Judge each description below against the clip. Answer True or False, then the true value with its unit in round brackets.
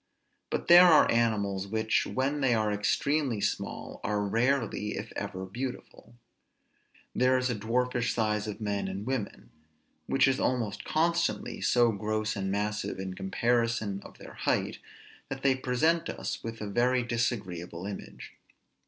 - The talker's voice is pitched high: False (115 Hz)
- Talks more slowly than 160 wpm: True (145 wpm)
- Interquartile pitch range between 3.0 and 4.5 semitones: True (3.7 semitones)